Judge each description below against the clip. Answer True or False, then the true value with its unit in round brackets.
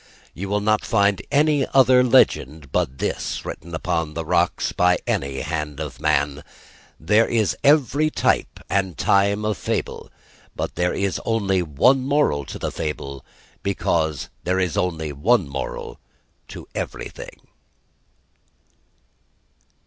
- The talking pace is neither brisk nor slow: False (130 wpm)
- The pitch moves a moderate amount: False (6.1 semitones)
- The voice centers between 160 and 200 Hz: False (90 Hz)